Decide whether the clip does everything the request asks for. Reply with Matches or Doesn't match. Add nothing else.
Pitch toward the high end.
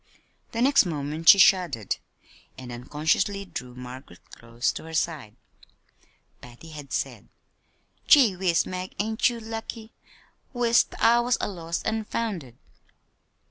Doesn't match